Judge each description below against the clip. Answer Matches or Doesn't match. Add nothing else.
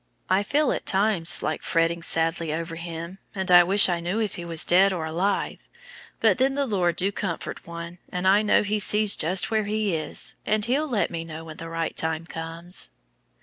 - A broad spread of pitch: Doesn't match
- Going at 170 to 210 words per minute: Matches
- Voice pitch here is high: Doesn't match